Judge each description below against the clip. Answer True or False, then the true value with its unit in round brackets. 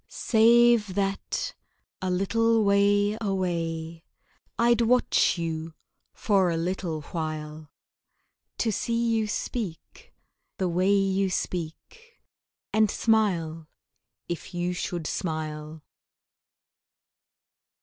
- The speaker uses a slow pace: True (90 wpm)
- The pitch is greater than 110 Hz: True (190 Hz)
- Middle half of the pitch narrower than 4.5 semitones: False (4.9 semitones)